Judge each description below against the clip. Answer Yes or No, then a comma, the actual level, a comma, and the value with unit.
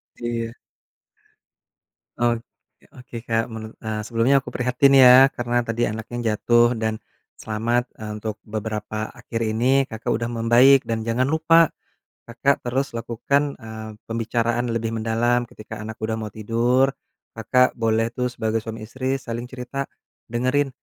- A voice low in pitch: Yes, low, 115 Hz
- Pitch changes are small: Yes, narrow, 2.1 semitones